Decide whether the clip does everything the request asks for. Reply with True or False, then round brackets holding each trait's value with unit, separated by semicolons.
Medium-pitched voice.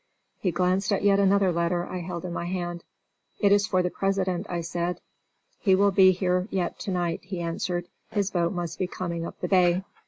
True (180 Hz)